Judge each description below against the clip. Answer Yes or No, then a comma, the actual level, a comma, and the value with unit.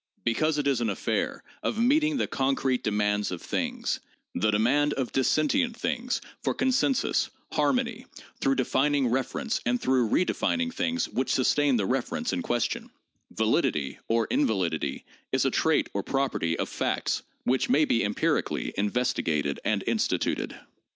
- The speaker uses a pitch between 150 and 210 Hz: No, low, 135 Hz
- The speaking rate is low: No, average, 150 wpm